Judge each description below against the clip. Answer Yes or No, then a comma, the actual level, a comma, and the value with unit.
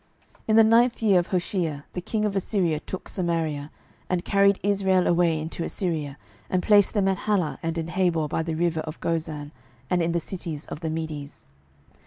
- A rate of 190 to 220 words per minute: Yes, average, 195 wpm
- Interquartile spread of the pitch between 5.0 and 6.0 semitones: No, average, 3.3 semitones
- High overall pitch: No, medium, 170 Hz